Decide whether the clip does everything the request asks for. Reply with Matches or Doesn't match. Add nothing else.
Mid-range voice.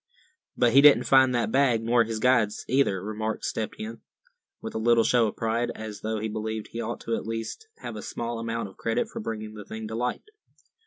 Doesn't match